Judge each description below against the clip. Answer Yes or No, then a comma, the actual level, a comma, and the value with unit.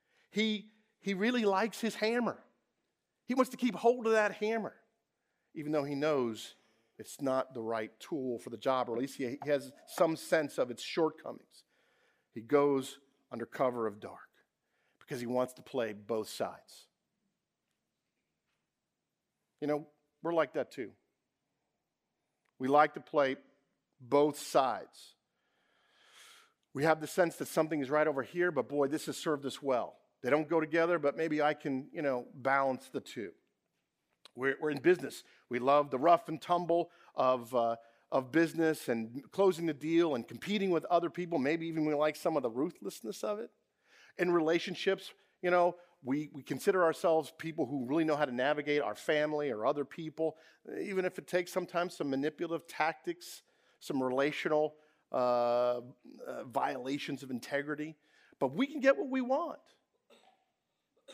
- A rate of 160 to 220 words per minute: Yes, average, 165 wpm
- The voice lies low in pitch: No, medium, 150 Hz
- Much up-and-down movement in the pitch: No, average, 4.4 semitones